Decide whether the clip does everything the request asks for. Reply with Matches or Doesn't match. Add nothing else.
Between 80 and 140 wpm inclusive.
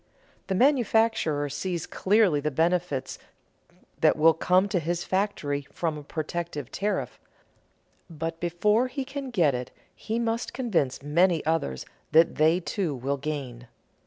Matches